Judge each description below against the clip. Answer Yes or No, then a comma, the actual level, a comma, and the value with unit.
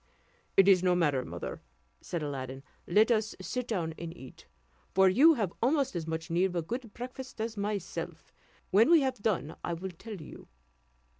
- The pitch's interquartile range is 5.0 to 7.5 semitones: Yes, wide, 5.6 semitones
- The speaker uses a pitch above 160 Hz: Yes, high, 190 Hz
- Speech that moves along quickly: No, average, 180 wpm